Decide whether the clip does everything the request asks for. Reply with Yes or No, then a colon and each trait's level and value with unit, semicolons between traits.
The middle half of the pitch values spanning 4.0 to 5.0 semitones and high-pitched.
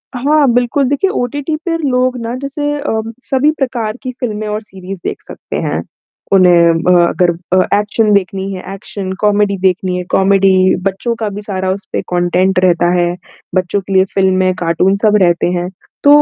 Yes: average, 4.7 semitones; high, 200 Hz